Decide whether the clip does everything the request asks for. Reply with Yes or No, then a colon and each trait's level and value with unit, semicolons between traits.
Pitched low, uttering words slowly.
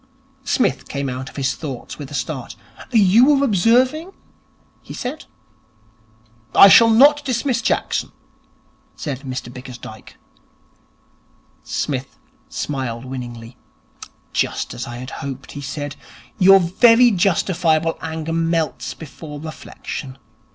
No: medium, 155 Hz; slow, 115 wpm